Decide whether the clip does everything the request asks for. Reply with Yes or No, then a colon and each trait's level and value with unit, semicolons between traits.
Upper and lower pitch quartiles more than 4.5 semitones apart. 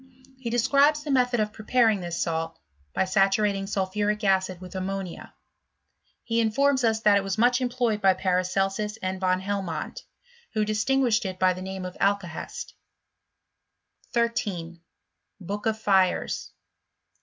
No: average, 3.3 semitones